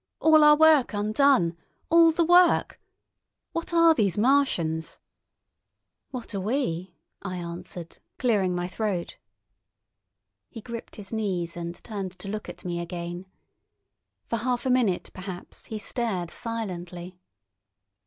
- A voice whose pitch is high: Yes, high, 205 Hz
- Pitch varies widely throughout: Yes, wide, 6.2 semitones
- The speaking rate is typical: No, slow, 125 wpm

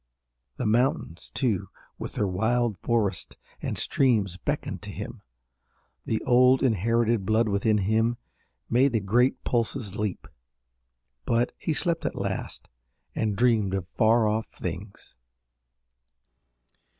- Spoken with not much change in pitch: No, average, 3.2 semitones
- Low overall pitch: Yes, low, 110 Hz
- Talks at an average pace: No, slow, 120 wpm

